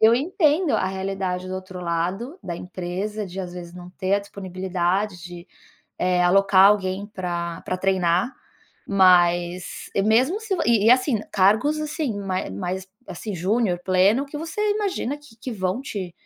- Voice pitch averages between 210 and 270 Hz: No, high, 190 Hz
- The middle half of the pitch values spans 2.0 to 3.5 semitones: No, average, 4.2 semitones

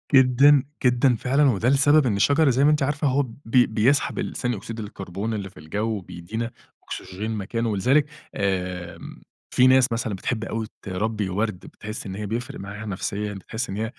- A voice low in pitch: Yes, low, 110 Hz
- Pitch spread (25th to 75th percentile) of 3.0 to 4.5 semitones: Yes, average, 4.2 semitones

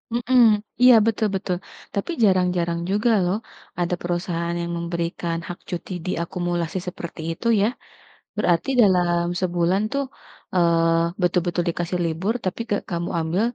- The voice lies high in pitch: No, medium, 175 Hz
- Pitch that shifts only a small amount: Yes, narrow, 1.9 semitones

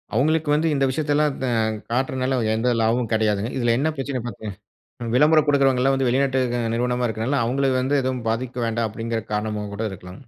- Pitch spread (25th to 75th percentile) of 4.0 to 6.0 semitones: No, average, 3.2 semitones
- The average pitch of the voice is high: No, low, 125 Hz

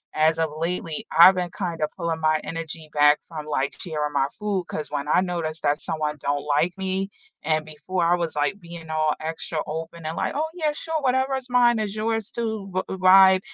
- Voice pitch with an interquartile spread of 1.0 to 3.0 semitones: No, average, 3.8 semitones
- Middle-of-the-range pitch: Yes, medium, 170 Hz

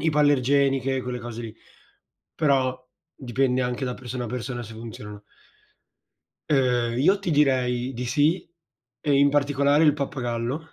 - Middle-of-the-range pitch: No, low, 130 Hz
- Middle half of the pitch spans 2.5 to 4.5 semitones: Yes, average, 2.8 semitones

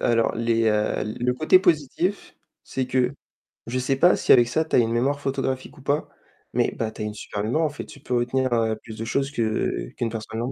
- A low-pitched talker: Yes, low, 125 Hz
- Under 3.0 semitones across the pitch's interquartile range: No, average, 3.5 semitones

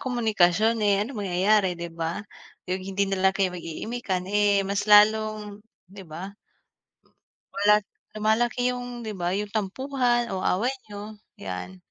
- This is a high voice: Yes, high, 205 Hz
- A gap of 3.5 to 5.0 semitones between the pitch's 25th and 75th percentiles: No, average, 2.7 semitones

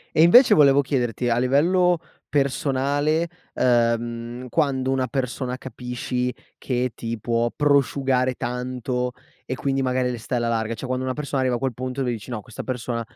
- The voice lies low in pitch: Yes, low, 130 Hz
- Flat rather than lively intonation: Yes, narrow, 2.2 semitones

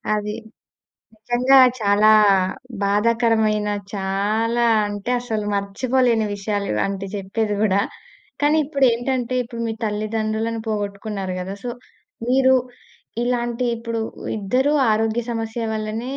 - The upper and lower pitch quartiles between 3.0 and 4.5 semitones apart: No, narrow, 2.5 semitones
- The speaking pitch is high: Yes, high, 220 Hz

